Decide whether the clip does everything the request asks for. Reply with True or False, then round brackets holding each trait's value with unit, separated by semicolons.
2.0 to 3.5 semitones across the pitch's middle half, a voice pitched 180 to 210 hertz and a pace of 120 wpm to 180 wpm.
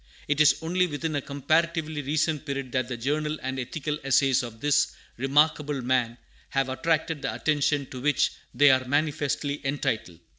False (2.5 semitones; 145 Hz; 160 wpm)